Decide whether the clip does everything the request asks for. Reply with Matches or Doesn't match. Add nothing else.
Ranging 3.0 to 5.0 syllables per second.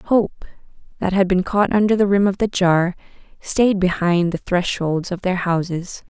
Matches